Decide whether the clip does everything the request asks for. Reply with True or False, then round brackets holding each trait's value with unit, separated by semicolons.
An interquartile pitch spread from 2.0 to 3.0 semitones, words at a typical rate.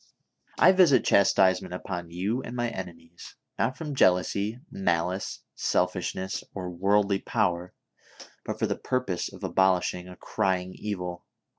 False (2.6 semitones; 130 wpm)